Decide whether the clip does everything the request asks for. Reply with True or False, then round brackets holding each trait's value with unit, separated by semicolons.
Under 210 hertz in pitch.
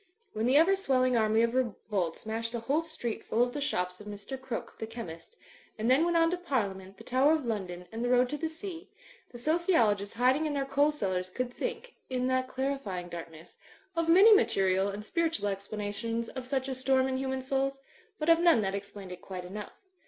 False (250 Hz)